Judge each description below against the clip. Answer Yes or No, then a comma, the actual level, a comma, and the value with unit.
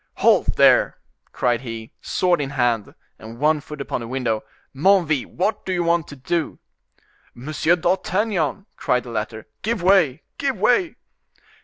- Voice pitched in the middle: Yes, medium, 150 Hz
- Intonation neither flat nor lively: No, wide, 6.7 semitones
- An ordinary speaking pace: Yes, average, 150 wpm